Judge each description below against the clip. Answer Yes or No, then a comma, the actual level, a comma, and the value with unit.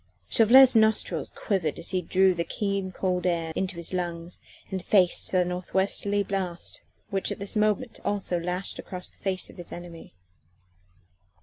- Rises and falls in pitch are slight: Yes, narrow, 2.2 semitones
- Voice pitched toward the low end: No, medium, 185 Hz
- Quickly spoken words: No, average, 160 wpm